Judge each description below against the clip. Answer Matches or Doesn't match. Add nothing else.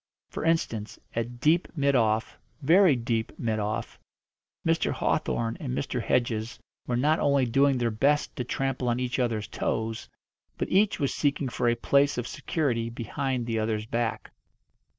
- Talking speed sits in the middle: Matches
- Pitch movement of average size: Matches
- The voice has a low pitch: Matches